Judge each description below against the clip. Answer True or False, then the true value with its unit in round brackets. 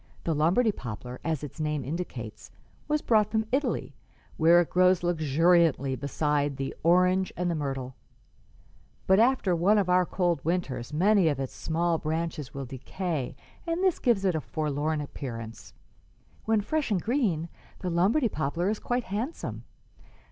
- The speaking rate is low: False (155 wpm)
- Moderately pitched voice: True (170 Hz)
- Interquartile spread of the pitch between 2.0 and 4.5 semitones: False (5.1 semitones)